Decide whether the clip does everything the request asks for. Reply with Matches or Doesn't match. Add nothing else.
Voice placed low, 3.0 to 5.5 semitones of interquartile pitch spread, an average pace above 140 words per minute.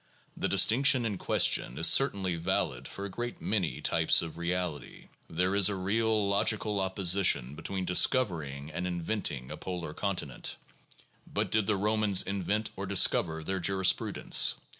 Matches